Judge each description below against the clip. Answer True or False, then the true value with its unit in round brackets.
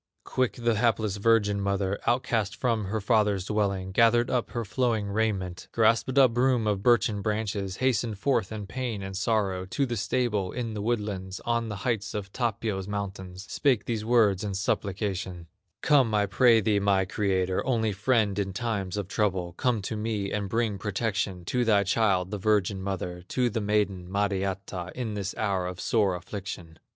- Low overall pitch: True (105 Hz)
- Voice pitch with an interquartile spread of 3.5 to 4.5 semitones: False (2.9 semitones)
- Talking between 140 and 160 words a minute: False (175 wpm)